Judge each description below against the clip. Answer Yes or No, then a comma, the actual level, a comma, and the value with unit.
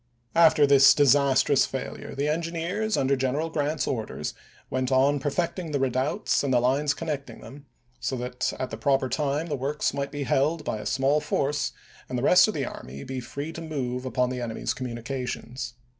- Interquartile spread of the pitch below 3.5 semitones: Yes, narrow, 2.6 semitones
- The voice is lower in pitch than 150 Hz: Yes, medium, 140 Hz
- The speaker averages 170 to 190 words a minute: Yes, average, 185 wpm